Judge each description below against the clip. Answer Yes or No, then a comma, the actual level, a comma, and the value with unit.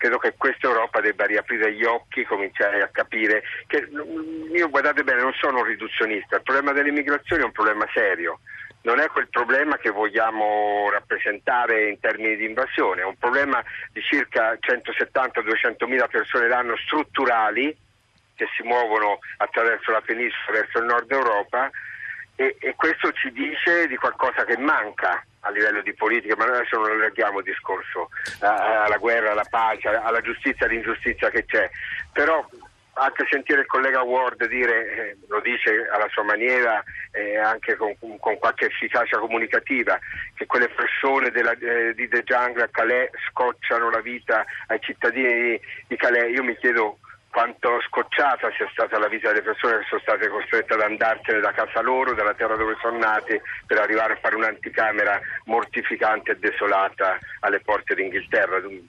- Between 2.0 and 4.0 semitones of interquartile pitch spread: Yes, average, 3.1 semitones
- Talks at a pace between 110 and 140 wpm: No, average, 165 wpm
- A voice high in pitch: No, low, 120 Hz